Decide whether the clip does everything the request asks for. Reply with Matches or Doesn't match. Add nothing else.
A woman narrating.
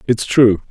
Doesn't match